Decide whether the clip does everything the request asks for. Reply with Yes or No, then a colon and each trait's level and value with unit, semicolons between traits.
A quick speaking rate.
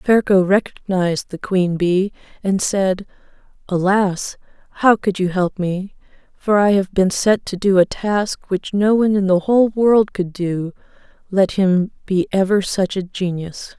No: average, 165 wpm